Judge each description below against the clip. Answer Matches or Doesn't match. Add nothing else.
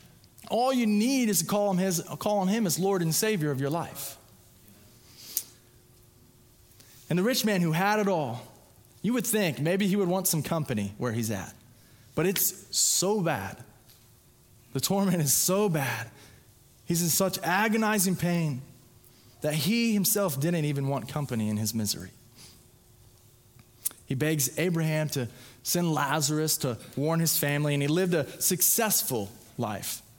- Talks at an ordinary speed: Matches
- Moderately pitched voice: Matches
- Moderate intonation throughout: Doesn't match